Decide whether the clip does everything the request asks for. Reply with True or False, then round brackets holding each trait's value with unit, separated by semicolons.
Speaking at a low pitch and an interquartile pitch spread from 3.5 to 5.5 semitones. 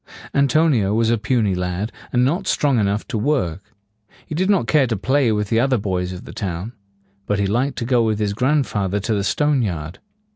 True (110 Hz; 5.0 semitones)